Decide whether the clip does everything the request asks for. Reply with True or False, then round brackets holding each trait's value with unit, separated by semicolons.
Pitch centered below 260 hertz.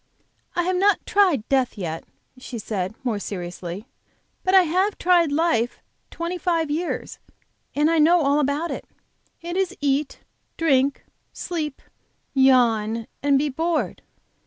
False (290 Hz)